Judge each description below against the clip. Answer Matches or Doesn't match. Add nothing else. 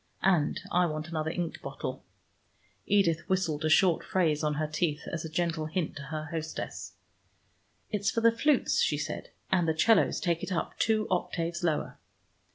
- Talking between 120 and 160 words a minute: Doesn't match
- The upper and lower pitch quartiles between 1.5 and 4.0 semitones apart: Matches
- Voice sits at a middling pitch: Matches